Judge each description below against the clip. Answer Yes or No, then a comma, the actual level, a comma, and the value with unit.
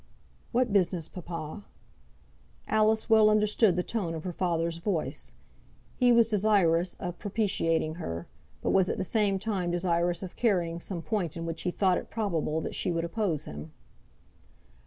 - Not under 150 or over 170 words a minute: Yes, average, 160 wpm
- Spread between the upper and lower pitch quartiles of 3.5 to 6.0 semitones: Yes, average, 4.1 semitones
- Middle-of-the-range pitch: Yes, medium, 180 Hz